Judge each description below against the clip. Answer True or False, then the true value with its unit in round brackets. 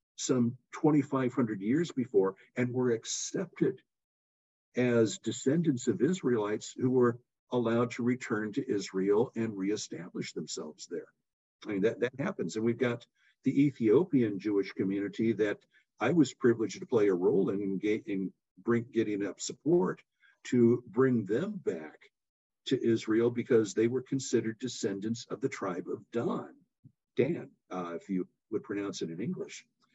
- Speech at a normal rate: True (150 wpm)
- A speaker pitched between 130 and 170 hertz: False (115 Hz)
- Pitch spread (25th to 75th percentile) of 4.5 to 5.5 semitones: False (3.6 semitones)